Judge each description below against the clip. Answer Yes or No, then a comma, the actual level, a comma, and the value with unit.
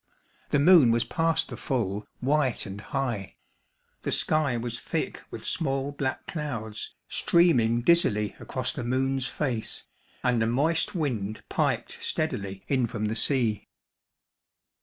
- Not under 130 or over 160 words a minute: Yes, slow, 135 wpm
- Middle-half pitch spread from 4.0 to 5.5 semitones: Yes, average, 4.6 semitones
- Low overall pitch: Yes, low, 125 Hz